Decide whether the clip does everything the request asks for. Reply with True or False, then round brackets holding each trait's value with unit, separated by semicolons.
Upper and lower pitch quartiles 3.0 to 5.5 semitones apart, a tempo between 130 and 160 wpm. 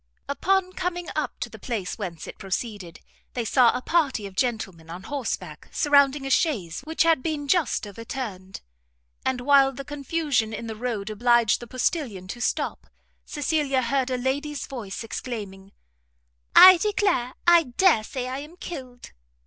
True (5.1 semitones; 155 wpm)